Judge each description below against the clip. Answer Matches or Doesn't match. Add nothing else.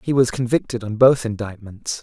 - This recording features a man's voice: Matches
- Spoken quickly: Doesn't match